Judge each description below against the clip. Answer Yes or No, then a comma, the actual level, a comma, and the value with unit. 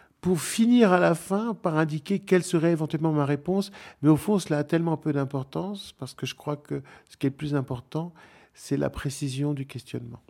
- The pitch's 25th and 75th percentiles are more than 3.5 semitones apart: Yes, average, 4.3 semitones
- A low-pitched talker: No, medium, 155 Hz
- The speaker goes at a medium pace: Yes, average, 210 wpm